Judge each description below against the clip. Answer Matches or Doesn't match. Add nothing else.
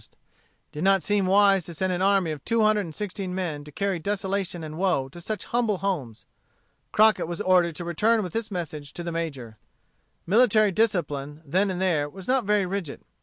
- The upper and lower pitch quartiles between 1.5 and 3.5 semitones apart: Doesn't match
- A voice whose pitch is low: Doesn't match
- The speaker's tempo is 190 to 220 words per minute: Matches